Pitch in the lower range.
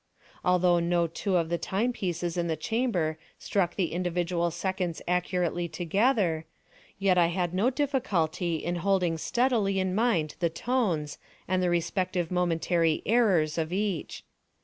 No: medium, 180 Hz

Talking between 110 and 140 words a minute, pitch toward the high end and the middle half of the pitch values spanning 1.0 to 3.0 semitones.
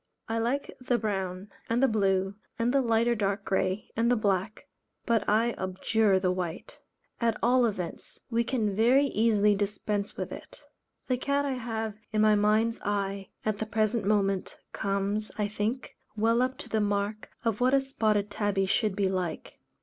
No: average, 175 wpm; high, 215 Hz; narrow, 2.6 semitones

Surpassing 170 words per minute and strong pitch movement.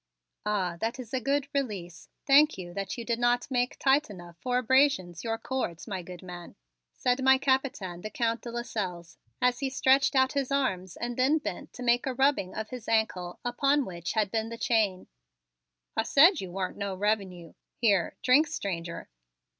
Yes: average, 185 wpm; wide, 5.8 semitones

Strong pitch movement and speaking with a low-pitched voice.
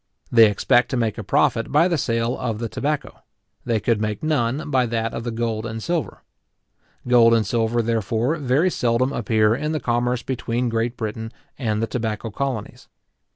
No: narrow, 2.4 semitones; low, 115 Hz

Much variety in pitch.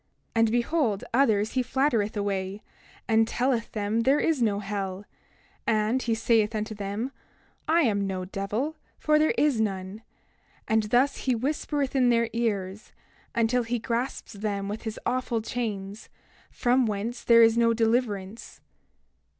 No: average, 3.1 semitones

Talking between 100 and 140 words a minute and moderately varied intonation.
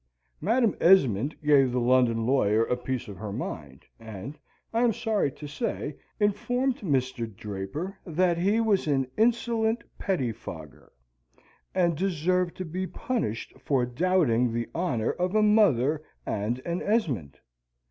No: slow, 135 wpm; wide, 8.4 semitones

